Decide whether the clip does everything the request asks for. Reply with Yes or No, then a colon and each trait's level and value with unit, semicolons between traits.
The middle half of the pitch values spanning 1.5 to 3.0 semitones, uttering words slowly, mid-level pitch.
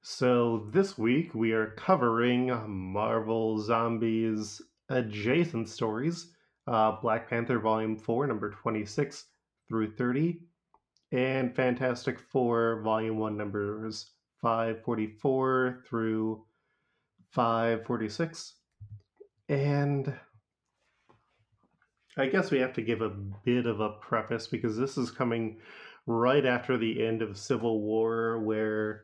No: average, 2.7 semitones; slow, 105 wpm; low, 115 Hz